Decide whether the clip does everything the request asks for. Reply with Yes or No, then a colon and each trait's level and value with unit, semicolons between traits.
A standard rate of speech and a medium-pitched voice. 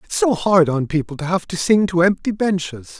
No: fast, 240 wpm; medium, 180 Hz